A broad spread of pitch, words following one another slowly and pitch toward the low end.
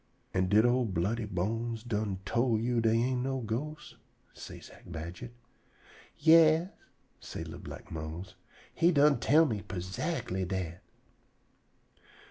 Yes: wide, 5.7 semitones; slow, 125 wpm; low, 115 Hz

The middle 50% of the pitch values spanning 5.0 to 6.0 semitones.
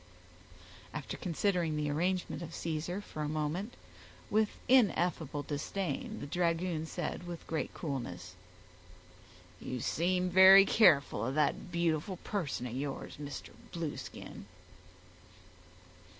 No: average, 3.9 semitones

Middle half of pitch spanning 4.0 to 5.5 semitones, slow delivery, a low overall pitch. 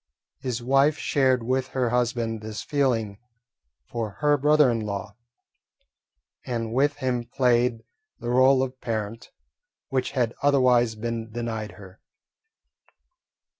No: narrow, 2.6 semitones; slow, 120 wpm; low, 120 Hz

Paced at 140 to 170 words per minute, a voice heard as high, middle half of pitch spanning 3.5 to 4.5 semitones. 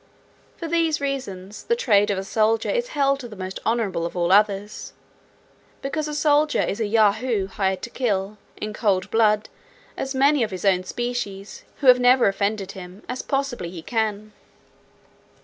No: average, 165 wpm; high, 215 Hz; average, 5.0 semitones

